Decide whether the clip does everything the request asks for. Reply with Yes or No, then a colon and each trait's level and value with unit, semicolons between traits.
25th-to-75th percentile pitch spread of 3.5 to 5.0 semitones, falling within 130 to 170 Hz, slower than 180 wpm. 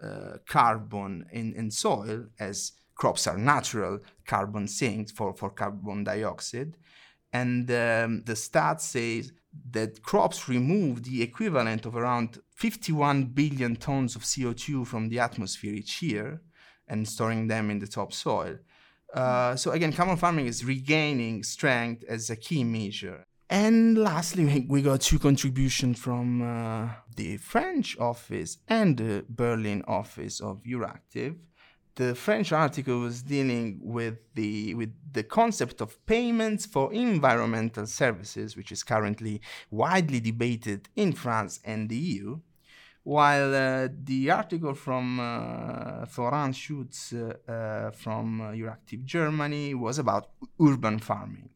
No: average, 4.5 semitones; low, 120 Hz; slow, 135 wpm